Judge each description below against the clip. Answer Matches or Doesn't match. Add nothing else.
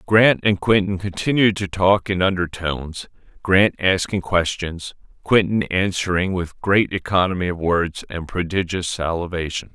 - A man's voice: Matches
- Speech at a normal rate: Doesn't match